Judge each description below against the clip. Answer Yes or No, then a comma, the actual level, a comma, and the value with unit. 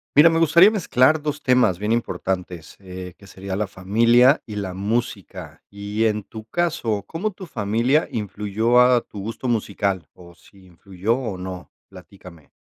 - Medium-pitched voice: No, low, 105 Hz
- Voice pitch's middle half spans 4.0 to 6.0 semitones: Yes, average, 4.8 semitones